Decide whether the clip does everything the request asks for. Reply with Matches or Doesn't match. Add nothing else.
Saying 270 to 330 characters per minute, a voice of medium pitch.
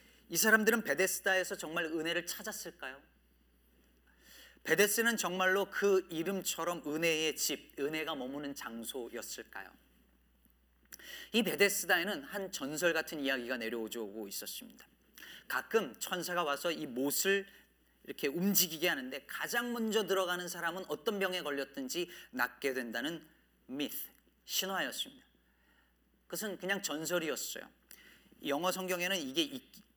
Matches